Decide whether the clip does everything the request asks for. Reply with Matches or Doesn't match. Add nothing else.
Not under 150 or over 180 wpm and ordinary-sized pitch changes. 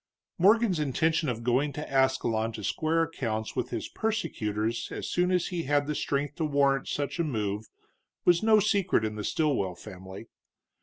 Doesn't match